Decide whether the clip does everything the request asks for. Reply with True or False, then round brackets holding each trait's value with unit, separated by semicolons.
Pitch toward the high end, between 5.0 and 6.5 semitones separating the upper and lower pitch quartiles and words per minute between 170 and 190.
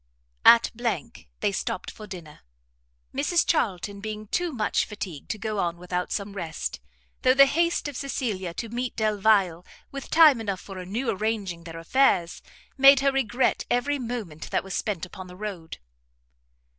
False (215 Hz; 5.3 semitones; 155 wpm)